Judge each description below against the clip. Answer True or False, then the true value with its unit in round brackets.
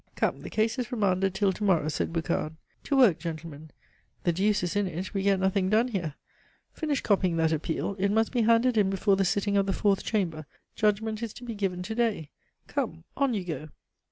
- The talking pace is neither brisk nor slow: False (215 wpm)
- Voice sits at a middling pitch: False (195 Hz)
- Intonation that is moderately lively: True (3.9 semitones)